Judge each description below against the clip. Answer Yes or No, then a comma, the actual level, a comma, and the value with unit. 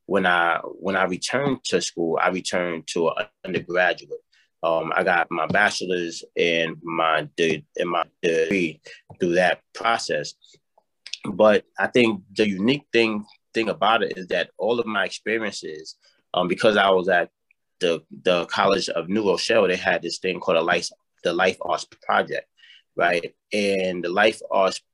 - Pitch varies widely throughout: Yes, wide, 8.0 semitones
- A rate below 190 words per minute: Yes, average, 165 wpm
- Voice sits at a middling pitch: No, low, 100 Hz